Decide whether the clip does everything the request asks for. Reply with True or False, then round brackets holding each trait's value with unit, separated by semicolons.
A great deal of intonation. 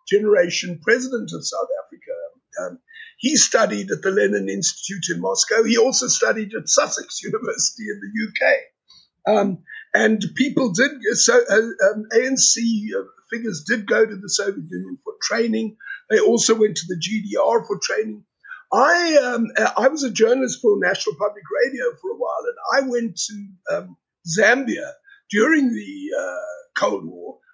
True (6.0 semitones)